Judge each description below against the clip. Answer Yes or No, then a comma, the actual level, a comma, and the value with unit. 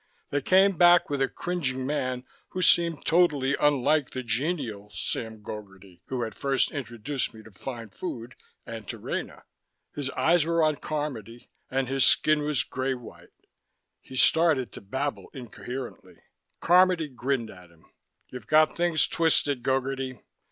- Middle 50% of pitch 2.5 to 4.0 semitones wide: No, average, 4.5 semitones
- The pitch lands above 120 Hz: Yes, low, 135 Hz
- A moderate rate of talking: Yes, average, 150 wpm